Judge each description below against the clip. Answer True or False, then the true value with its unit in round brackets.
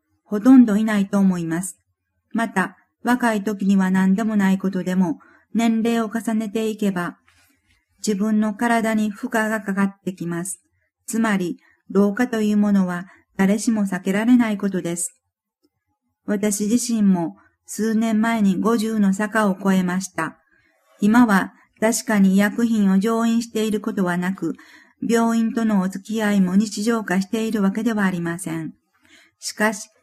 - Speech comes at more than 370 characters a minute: False (280 characters per minute)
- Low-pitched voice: False (210 Hz)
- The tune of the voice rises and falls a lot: False (3.0 semitones)